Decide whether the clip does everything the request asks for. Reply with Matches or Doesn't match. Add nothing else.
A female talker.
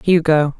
Matches